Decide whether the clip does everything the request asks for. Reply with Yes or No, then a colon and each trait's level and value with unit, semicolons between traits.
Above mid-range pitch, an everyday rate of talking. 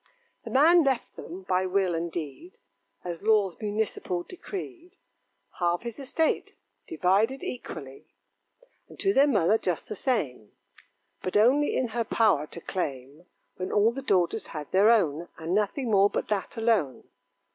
Yes: high, 205 Hz; average, 150 wpm